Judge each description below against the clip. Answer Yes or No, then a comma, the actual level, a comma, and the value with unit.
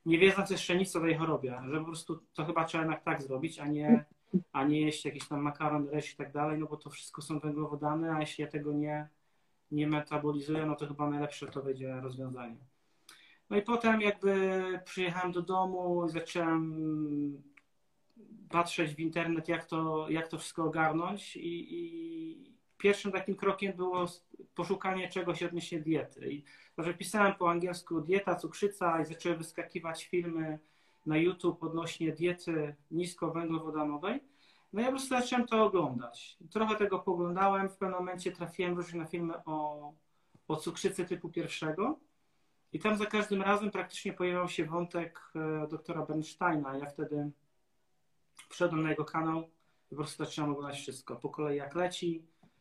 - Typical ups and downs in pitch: Yes, average, 3.2 semitones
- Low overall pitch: No, medium, 165 Hz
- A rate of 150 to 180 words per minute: Yes, fast, 160 wpm